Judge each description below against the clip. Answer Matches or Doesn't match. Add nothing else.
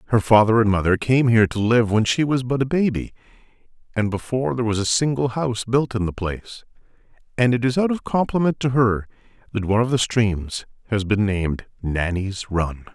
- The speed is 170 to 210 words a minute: Matches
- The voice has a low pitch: Matches